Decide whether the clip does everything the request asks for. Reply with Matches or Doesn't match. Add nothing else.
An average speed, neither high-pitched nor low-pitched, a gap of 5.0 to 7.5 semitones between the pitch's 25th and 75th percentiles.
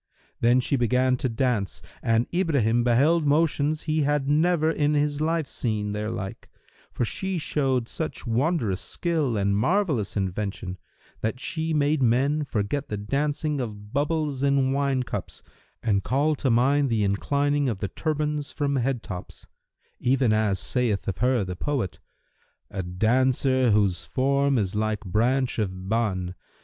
Doesn't match